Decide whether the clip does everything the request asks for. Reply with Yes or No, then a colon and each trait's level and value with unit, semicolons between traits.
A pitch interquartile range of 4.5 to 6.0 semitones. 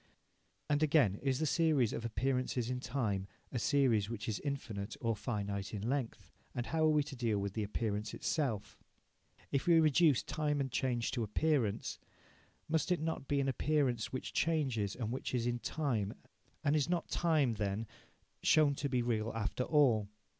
Yes: average, 5.0 semitones